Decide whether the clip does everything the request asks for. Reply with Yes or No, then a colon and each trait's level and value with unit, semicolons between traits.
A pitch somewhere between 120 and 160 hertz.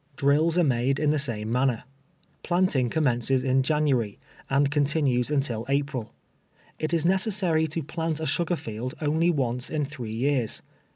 Yes: medium, 140 Hz